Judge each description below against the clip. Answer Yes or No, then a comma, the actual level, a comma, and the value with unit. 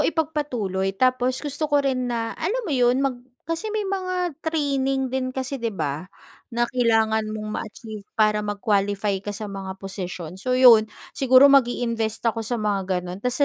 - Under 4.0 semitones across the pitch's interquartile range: No, average, 4.6 semitones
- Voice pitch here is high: Yes, high, 240 Hz